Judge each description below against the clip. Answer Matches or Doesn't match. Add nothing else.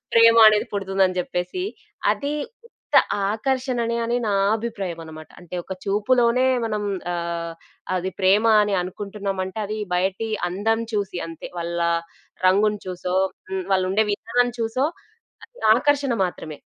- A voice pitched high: Matches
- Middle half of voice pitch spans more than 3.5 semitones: Matches